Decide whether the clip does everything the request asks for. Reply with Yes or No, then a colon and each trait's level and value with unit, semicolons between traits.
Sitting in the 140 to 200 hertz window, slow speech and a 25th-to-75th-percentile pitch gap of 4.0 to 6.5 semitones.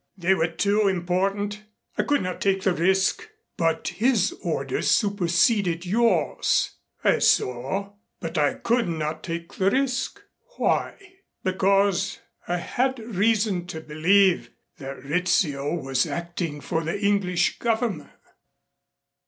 No: medium, 185 Hz; slow, 120 wpm; average, 3.5 semitones